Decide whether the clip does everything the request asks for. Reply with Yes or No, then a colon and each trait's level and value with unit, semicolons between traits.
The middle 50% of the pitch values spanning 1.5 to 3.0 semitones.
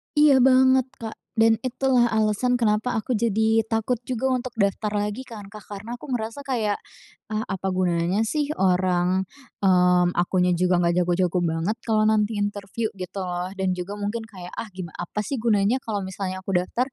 No: average, 3.9 semitones